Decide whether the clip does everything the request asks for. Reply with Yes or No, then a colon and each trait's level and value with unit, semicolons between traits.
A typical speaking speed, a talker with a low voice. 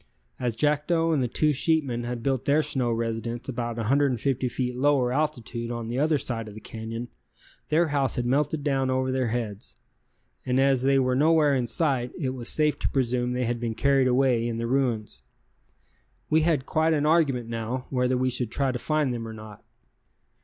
Yes: average, 195 wpm; low, 130 Hz